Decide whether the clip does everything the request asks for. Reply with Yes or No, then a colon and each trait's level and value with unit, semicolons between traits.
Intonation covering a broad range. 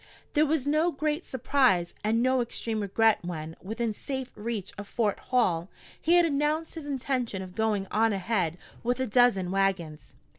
Yes: wide, 5.7 semitones